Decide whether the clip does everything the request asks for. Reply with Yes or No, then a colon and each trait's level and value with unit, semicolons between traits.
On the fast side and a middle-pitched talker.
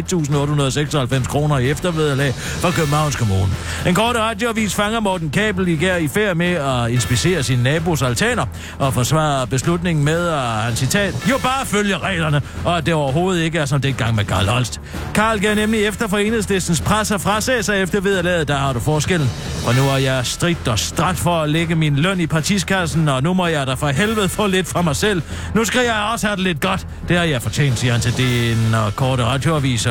No: average, 215 wpm; medium, 160 Hz